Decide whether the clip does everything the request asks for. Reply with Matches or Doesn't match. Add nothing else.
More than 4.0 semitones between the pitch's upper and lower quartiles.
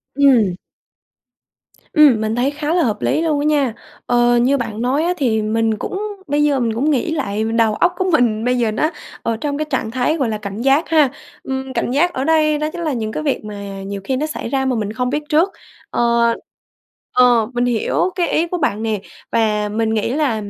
Matches